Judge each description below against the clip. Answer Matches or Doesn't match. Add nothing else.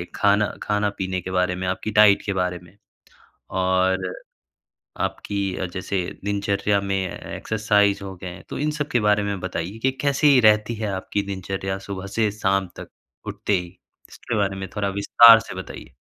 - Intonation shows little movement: Matches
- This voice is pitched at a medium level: Doesn't match